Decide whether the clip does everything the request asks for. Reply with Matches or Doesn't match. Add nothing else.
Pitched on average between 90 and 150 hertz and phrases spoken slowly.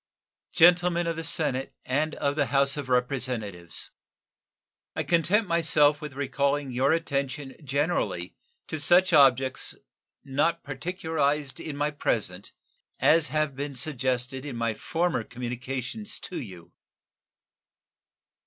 Matches